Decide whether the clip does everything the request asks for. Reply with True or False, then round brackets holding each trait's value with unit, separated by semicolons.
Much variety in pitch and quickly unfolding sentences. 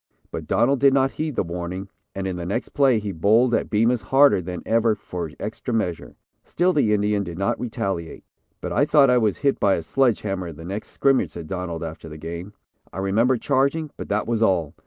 True (5.9 semitones; 220 wpm)